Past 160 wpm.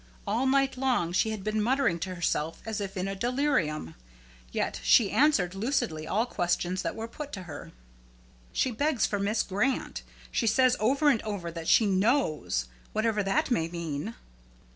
Yes: average, 170 wpm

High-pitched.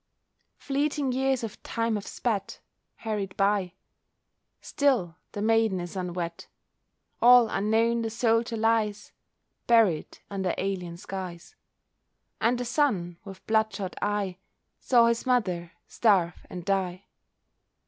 Yes: high, 210 Hz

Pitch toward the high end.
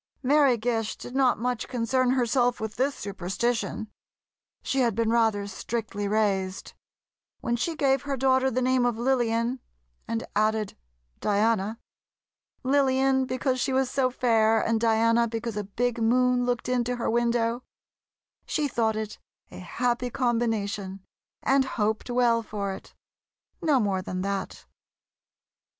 Yes: high, 235 Hz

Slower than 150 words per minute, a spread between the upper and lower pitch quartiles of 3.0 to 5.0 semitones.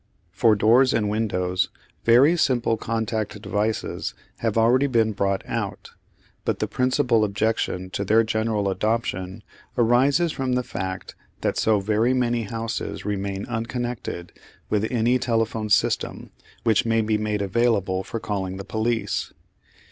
No: slow, 135 wpm; narrow, 2.6 semitones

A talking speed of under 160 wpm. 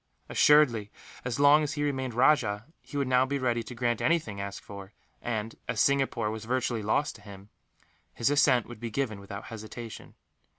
No: average, 180 wpm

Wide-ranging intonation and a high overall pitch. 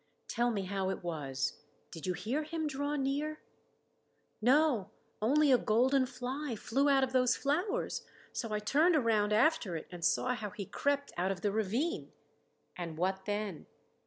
Yes: wide, 6.5 semitones; high, 240 Hz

